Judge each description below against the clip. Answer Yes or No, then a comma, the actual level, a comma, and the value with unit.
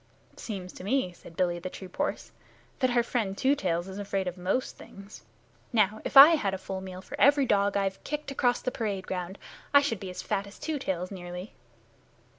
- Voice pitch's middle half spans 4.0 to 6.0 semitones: Yes, average, 4.8 semitones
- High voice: Yes, high, 195 Hz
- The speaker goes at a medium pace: No, fast, 215 wpm